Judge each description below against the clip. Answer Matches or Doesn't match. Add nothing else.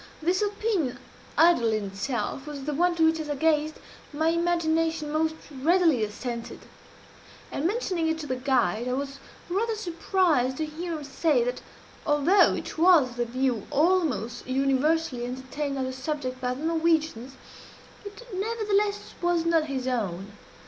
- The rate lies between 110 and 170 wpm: Matches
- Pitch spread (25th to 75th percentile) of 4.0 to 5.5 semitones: Matches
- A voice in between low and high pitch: Doesn't match